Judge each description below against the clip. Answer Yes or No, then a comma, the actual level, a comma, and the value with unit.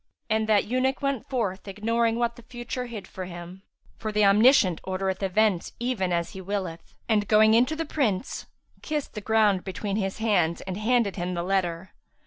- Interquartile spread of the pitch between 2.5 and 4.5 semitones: Yes, average, 3.8 semitones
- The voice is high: Yes, high, 210 Hz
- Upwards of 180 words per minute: Yes, average, 190 wpm